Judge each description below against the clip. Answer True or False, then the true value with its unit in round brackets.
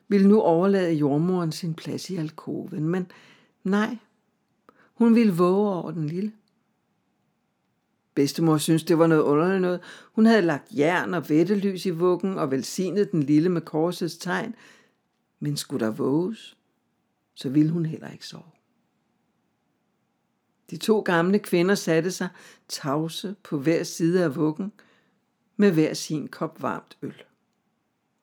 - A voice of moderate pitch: True (180 Hz)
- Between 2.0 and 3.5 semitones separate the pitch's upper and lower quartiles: False (4.2 semitones)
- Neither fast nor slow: False (140 wpm)